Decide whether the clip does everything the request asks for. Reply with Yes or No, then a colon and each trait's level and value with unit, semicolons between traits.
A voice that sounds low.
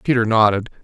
Yes: low, 115 Hz